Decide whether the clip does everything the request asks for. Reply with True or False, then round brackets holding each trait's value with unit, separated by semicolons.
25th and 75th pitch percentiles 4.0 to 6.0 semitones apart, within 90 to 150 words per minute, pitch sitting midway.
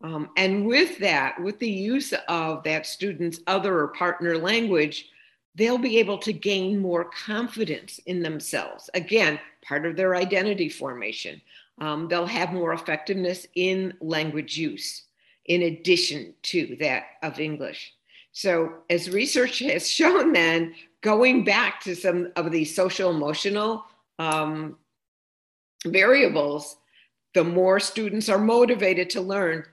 True (4.5 semitones; 135 wpm; 180 Hz)